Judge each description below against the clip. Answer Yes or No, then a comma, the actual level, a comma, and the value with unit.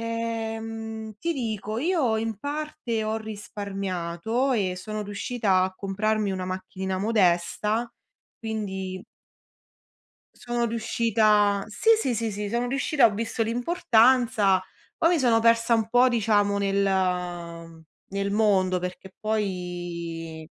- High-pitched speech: Yes, high, 215 Hz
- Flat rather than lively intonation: No, average, 3.3 semitones